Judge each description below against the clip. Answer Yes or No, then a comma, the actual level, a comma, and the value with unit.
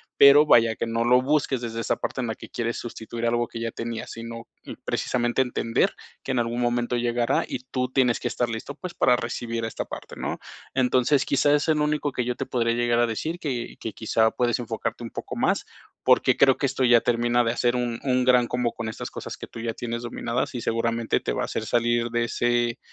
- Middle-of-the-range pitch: No, low, 120 Hz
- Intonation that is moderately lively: No, narrow, 1.4 semitones